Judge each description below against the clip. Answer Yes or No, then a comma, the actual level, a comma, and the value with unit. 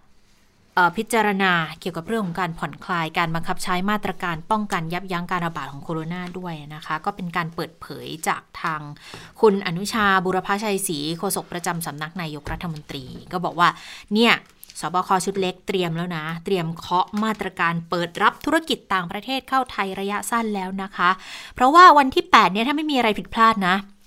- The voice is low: No, medium, 185 Hz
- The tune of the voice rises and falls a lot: No, average, 3.3 semitones